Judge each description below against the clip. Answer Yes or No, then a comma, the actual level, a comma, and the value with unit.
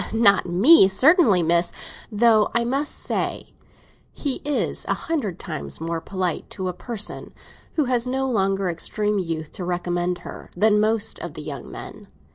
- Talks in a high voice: Yes, high, 200 Hz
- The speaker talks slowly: No, average, 160 wpm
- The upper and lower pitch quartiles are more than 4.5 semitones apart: Yes, average, 5.2 semitones